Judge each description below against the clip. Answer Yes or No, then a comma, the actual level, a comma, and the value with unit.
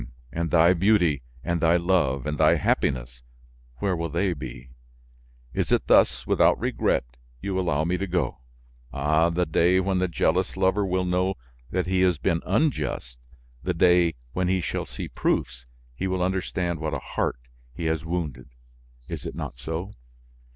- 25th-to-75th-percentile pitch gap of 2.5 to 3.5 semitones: Yes, average, 3.0 semitones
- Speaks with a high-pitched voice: No, very low, 85 Hz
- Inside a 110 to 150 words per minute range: No, average, 165 wpm